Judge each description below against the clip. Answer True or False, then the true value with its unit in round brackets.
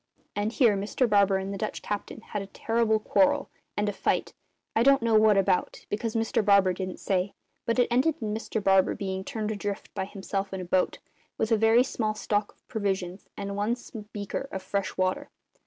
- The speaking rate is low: False (195 wpm)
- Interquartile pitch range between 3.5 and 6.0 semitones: False (2.4 semitones)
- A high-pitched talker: True (205 Hz)